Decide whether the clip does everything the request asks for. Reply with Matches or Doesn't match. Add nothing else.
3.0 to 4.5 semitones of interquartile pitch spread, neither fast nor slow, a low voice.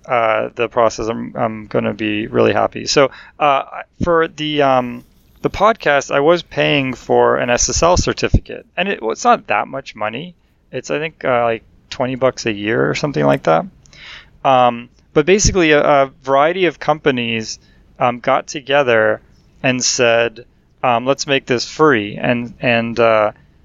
Matches